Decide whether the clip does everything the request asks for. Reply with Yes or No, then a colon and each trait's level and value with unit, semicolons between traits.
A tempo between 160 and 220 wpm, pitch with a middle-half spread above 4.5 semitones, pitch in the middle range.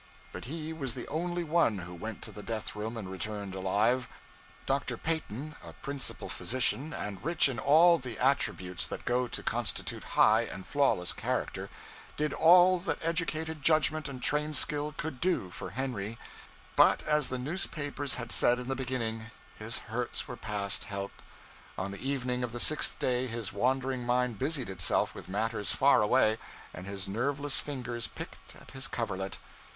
No: average, 170 wpm; average, 5.2 semitones; low, 125 Hz